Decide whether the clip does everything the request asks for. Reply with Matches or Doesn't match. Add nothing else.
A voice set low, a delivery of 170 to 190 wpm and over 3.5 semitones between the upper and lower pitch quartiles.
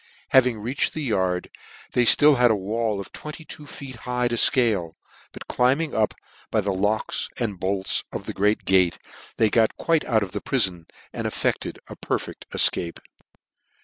Matches